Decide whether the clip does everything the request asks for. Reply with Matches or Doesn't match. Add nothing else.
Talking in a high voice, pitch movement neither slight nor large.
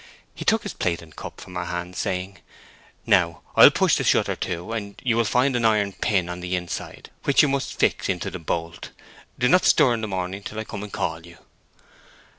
Doesn't match